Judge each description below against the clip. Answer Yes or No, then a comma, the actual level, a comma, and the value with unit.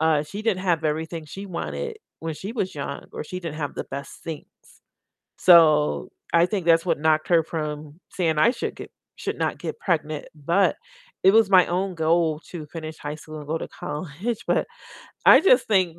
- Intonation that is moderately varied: Yes, average, 3.3 semitones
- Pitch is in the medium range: Yes, medium, 165 Hz